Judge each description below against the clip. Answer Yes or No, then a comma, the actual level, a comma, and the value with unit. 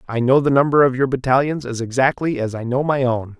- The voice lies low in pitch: Yes, low, 130 Hz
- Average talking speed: No, fast, 245 wpm